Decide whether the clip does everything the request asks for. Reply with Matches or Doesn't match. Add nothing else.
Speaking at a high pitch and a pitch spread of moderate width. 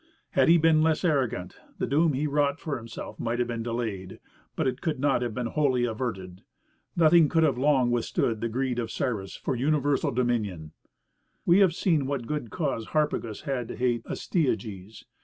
Doesn't match